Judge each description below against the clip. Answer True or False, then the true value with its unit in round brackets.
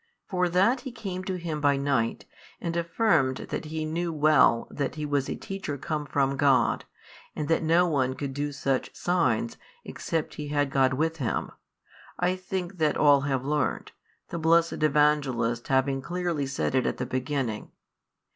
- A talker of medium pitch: True (150 Hz)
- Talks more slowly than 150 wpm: False (170 wpm)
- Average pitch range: True (3.8 semitones)